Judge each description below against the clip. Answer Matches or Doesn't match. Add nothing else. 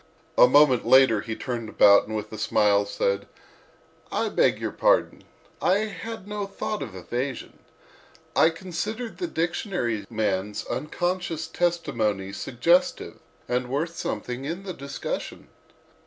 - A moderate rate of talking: Doesn't match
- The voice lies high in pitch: Doesn't match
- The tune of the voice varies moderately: Doesn't match